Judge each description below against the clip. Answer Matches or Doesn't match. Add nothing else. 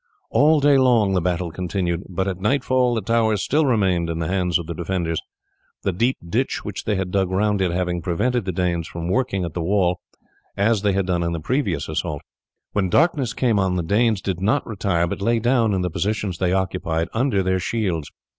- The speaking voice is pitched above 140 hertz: Doesn't match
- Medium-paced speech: Doesn't match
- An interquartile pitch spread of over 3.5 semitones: Matches